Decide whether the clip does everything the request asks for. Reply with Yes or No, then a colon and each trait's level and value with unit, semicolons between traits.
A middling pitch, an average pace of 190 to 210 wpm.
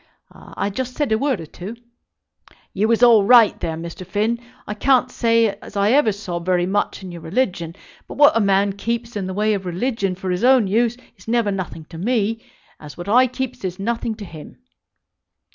No: high, 210 Hz; fast, 205 wpm